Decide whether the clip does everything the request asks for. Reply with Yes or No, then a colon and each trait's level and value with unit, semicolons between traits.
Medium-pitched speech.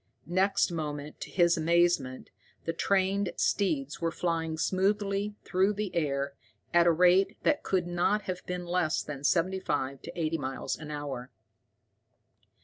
Yes: medium, 170 Hz